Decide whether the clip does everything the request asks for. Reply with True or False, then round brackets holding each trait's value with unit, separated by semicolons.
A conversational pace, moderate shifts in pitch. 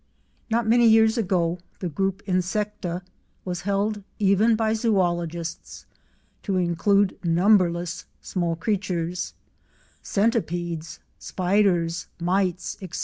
False (90 wpm; 3.3 semitones)